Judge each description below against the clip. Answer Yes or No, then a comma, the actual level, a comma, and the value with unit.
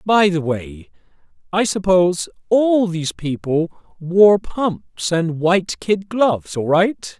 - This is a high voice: No, medium, 175 Hz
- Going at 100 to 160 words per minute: Yes, slow, 135 wpm